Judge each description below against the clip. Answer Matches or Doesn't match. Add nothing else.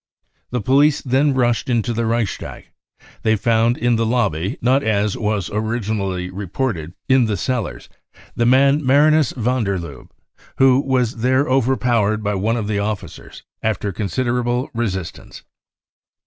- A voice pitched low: Matches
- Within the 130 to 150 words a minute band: Matches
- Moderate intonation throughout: Matches